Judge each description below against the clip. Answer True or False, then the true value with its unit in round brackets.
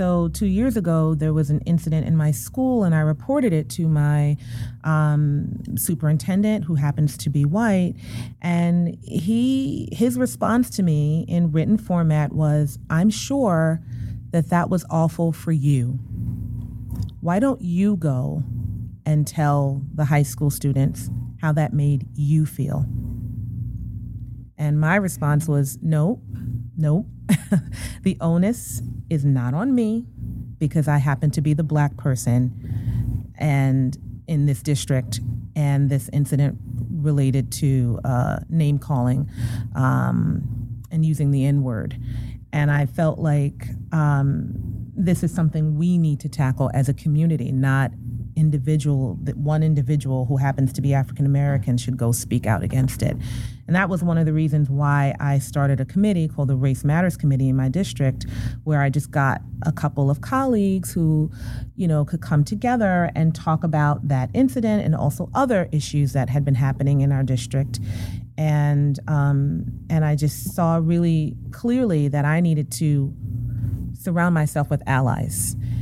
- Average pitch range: True (4.2 semitones)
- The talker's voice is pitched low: False (145 Hz)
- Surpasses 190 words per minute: False (155 wpm)